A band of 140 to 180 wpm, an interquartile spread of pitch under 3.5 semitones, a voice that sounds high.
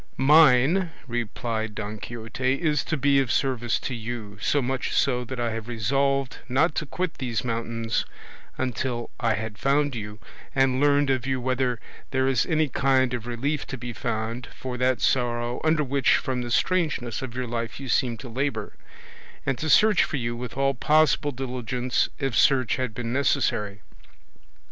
No: average, 170 wpm; narrow, 2.6 semitones; low, 125 Hz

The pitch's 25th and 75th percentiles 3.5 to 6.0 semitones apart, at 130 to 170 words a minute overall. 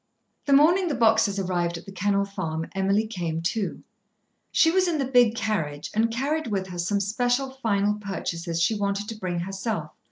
No: average, 4.3 semitones; average, 185 wpm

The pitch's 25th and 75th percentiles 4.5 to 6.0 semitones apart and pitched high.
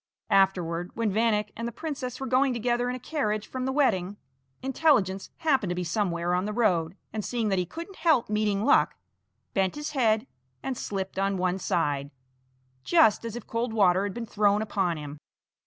Yes: average, 4.8 semitones; high, 210 Hz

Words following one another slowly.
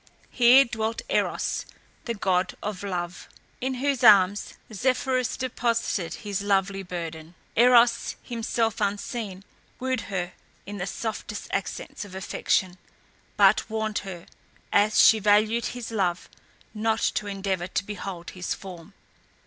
Yes: slow, 125 wpm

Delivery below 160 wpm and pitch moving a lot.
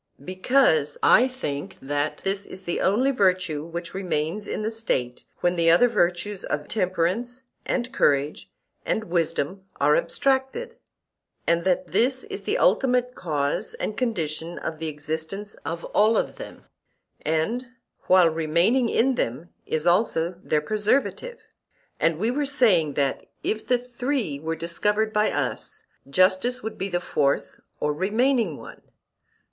Yes: average, 145 wpm; wide, 6.7 semitones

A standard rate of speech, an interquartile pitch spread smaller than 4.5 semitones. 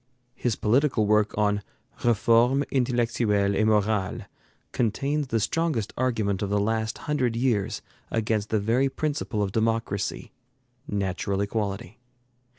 No: slow, 120 wpm; average, 3.1 semitones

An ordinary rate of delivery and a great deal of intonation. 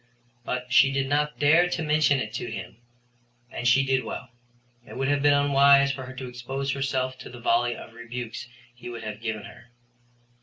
No: average, 195 wpm; narrow, 2.6 semitones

